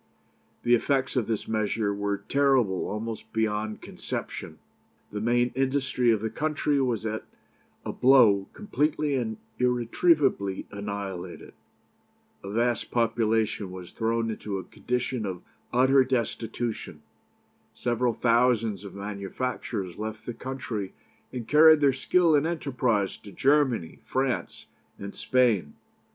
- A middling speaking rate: No, slow, 120 wpm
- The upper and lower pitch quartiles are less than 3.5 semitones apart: No, average, 4.0 semitones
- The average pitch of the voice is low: Yes, low, 115 Hz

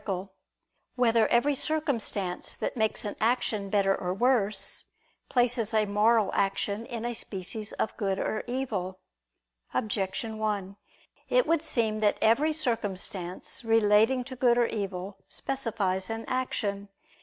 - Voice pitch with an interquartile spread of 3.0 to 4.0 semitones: Yes, average, 3.3 semitones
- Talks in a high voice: Yes, high, 220 Hz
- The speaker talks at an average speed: No, slow, 130 wpm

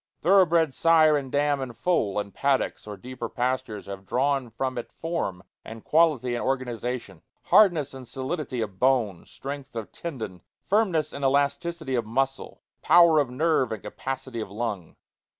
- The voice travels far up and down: No, average, 4.9 semitones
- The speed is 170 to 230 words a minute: No, average, 160 wpm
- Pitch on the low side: Yes, low, 130 Hz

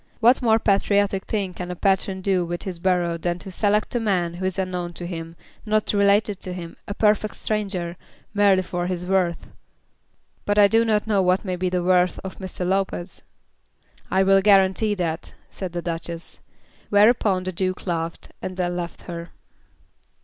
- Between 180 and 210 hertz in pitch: Yes, medium, 185 Hz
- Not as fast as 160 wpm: No, average, 180 wpm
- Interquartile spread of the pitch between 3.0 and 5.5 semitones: No, narrow, 2.4 semitones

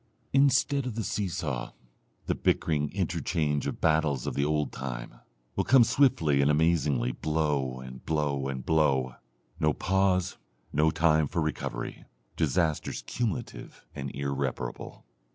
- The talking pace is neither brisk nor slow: No, slow, 130 wpm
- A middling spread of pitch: Yes, average, 3.6 semitones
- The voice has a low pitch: Yes, very low, 75 Hz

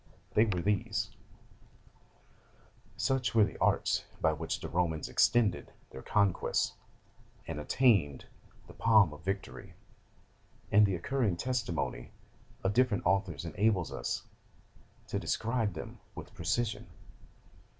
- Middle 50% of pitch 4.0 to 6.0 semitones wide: Yes, average, 5.0 semitones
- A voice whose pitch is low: Yes, low, 100 Hz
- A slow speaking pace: Yes, slow, 115 wpm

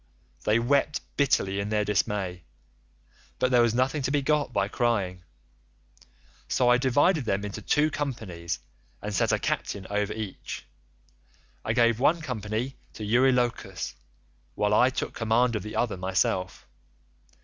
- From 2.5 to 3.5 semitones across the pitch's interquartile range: No, average, 4.1 semitones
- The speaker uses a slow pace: No, average, 145 wpm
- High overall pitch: No, low, 115 Hz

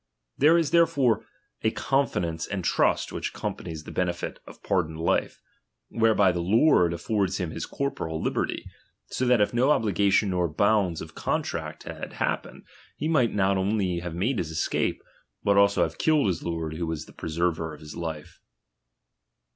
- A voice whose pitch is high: No, very low, 95 Hz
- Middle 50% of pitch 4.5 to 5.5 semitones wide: Yes, average, 5.1 semitones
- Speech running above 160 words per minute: Yes, average, 170 wpm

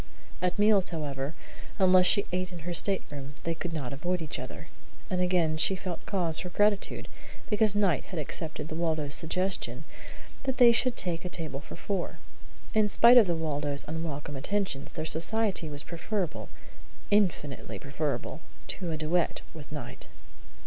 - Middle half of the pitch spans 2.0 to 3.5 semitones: No, average, 3.9 semitones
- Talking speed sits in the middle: Yes, average, 160 wpm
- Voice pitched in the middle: Yes, medium, 170 Hz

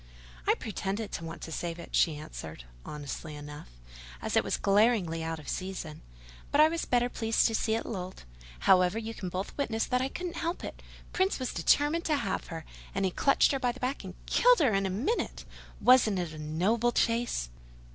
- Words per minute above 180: Yes, fast, 205 wpm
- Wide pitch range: Yes, wide, 7.1 semitones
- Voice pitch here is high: Yes, high, 210 Hz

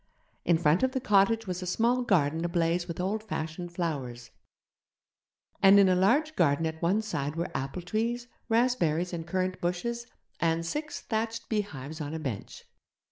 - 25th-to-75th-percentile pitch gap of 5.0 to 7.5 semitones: Yes, wide, 5.4 semitones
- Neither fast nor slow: Yes, average, 165 wpm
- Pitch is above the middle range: No, medium, 180 Hz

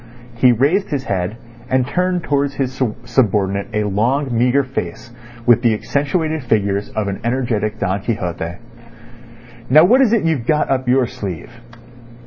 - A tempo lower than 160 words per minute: Yes, average, 150 wpm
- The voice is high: No, low, 125 Hz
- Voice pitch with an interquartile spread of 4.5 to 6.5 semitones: Yes, average, 5.1 semitones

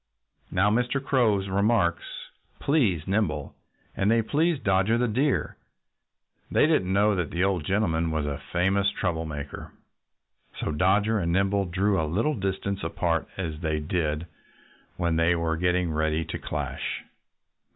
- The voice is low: Yes, very low, 95 Hz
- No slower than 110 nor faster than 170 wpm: Yes, average, 150 wpm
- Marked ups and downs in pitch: No, average, 4.2 semitones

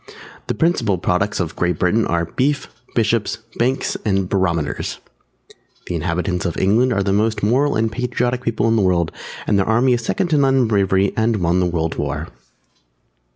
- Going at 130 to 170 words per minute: No, average, 180 wpm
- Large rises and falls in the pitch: No, average, 4.8 semitones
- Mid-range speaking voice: No, low, 105 Hz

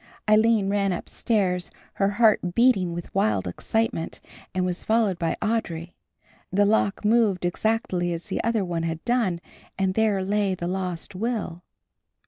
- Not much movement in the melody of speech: No, average, 3.8 semitones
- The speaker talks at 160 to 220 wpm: No, average, 145 wpm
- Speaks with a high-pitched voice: Yes, high, 195 Hz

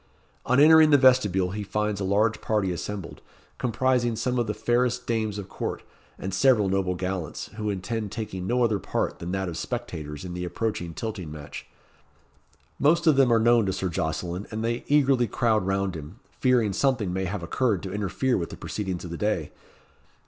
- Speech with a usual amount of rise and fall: Yes, average, 4.5 semitones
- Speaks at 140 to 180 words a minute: No, average, 190 wpm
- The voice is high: No, low, 105 Hz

